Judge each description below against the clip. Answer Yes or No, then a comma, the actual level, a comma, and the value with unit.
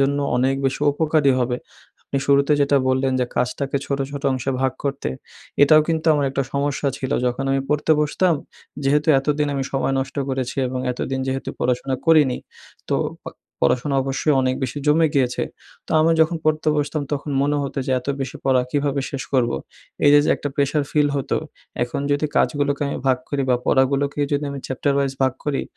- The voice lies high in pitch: No, medium, 140 Hz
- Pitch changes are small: Yes, narrow, 1.7 semitones